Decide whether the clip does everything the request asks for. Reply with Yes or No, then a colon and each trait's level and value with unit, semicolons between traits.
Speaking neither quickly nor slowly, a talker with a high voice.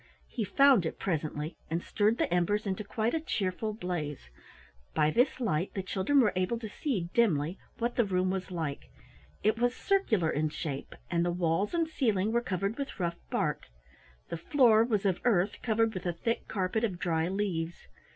Yes: average, 185 wpm; high, 195 Hz